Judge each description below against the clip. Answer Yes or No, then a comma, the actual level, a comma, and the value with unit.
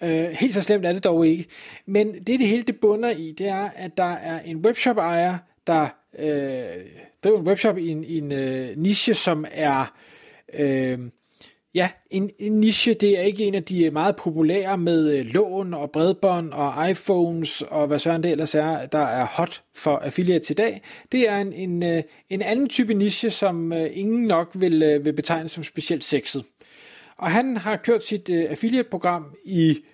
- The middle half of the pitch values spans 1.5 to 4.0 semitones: No, average, 4.5 semitones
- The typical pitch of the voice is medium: Yes, medium, 175 Hz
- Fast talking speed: No, average, 180 wpm